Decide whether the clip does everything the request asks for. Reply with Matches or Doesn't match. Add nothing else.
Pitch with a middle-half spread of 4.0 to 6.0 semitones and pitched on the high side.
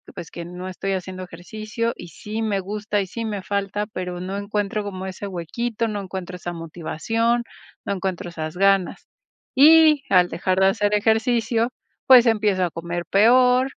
Doesn't match